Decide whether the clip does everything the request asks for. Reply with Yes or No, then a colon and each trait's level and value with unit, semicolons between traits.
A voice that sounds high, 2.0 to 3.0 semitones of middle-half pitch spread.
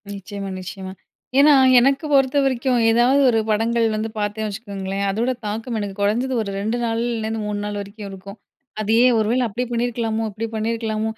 Yes: high, 220 Hz; narrow, 2.6 semitones